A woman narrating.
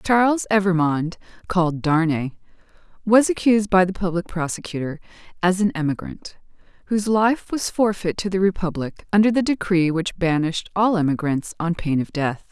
Yes: female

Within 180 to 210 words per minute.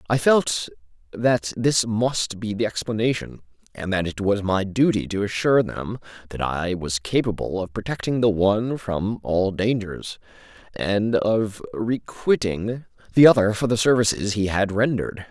No: average, 155 wpm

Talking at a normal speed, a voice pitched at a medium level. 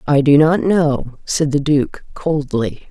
Yes: average, 165 wpm; medium, 145 Hz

